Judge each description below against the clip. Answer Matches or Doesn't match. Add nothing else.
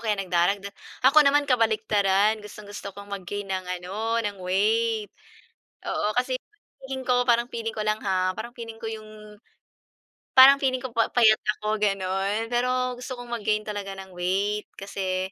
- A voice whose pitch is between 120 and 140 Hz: Doesn't match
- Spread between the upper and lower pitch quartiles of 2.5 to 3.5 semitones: Matches